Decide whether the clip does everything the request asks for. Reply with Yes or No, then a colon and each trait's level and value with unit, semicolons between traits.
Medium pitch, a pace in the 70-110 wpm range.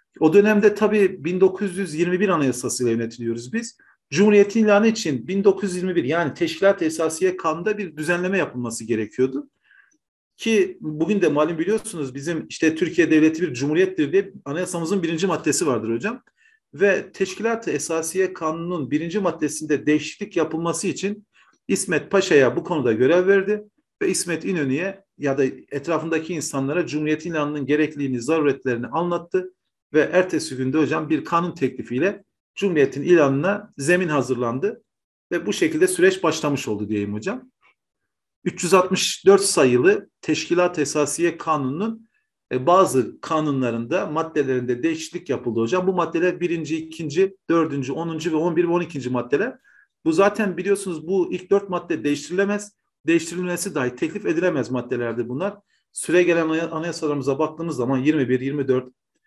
No: medium, 165 Hz; average, 130 wpm